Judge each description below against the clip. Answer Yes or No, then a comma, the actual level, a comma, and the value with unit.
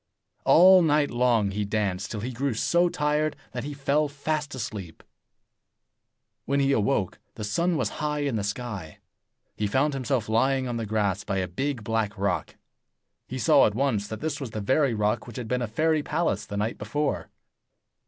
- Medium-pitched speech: No, low, 125 Hz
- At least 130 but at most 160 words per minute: No, average, 185 wpm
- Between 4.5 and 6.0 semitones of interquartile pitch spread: Yes, wide, 5.5 semitones